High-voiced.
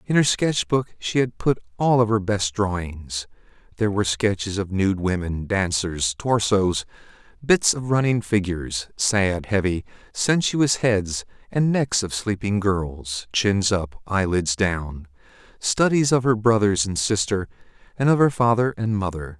No: low, 105 Hz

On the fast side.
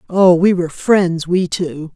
No: average, 185 wpm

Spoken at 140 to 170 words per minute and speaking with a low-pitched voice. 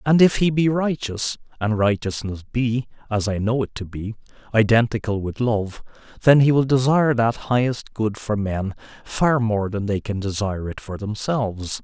Yes: average, 165 wpm; low, 115 Hz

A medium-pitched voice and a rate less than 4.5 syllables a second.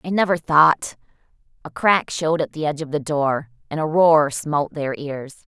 No: medium, 150 Hz; 5.0 syllables/s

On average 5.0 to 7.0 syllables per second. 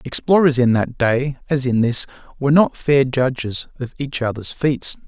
No: 4.6 syllables/s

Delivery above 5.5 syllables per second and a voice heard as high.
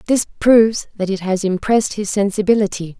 Yes: 5.8 syllables/s; high, 205 Hz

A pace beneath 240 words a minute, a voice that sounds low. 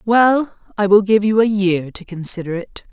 No: fast, 205 wpm; high, 200 Hz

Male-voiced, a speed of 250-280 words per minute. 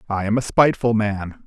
No: male; fast, 205 wpm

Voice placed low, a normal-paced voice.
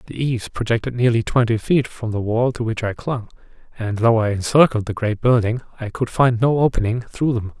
No: low, 115 Hz; fast, 215 wpm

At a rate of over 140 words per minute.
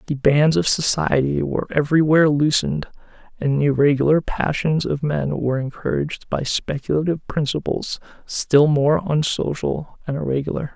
No: slow, 135 wpm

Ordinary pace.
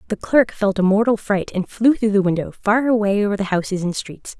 No: fast, 245 wpm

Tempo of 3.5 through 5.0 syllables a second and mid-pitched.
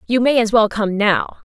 No: 4.7 syllables/s; high, 220 Hz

